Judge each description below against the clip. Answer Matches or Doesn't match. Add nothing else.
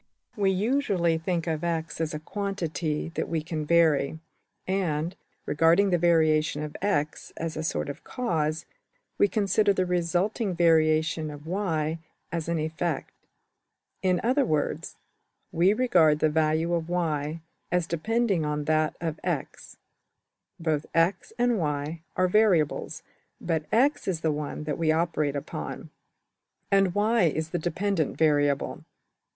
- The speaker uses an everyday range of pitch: Matches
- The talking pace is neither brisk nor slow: Doesn't match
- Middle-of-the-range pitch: Matches